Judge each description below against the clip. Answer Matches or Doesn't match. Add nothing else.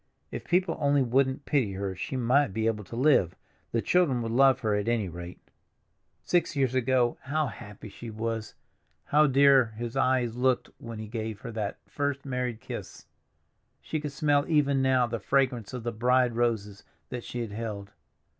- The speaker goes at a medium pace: Matches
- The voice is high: Doesn't match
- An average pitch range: Matches